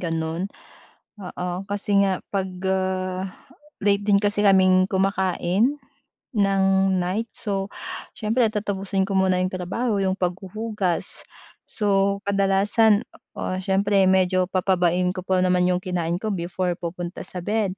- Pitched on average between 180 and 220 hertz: Yes, high, 190 Hz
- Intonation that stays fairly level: Yes, narrow, 1.6 semitones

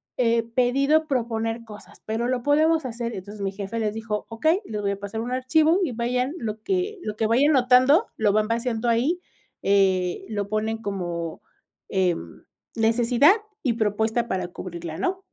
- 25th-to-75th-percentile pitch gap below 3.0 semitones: No, average, 3.6 semitones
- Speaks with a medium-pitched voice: No, high, 230 Hz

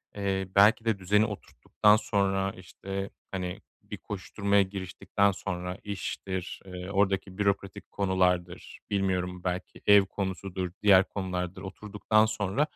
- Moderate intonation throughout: No, narrow, 1.6 semitones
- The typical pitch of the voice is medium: No, very low, 95 Hz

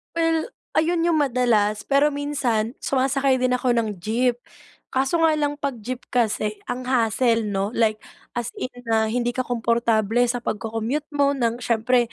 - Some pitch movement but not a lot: Yes, average, 3.5 semitones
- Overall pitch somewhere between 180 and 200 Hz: No, high, 245 Hz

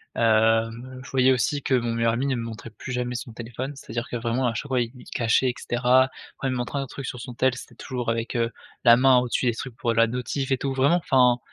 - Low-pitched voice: Yes, low, 125 Hz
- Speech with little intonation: Yes, narrow, 2.1 semitones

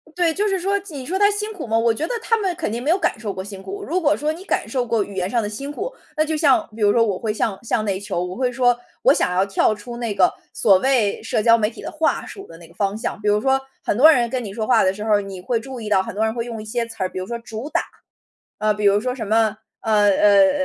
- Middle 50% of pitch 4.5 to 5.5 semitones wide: Yes, average, 5.1 semitones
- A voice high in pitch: Yes, high, 230 Hz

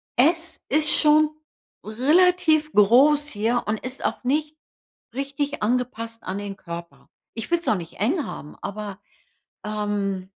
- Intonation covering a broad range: Yes, wide, 6.4 semitones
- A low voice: No, high, 245 Hz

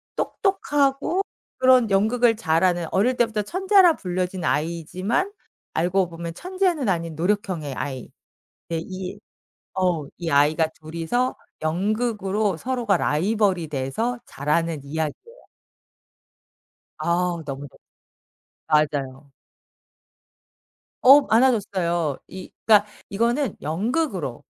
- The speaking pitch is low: No, medium, 185 Hz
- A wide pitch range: Yes, wide, 6.8 semitones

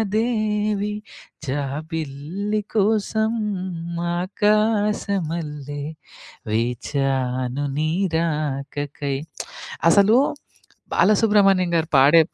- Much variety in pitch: Yes, wide, 6.6 semitones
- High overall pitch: No, medium, 165 Hz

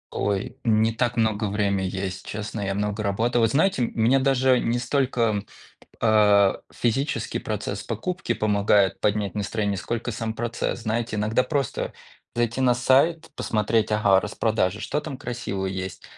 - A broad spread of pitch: No, average, 3.0 semitones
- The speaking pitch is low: Yes, low, 110 Hz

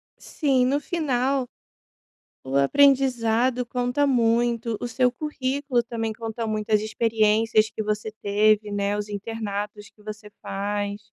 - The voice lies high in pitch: Yes, high, 225 Hz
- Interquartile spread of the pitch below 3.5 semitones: Yes, average, 3.0 semitones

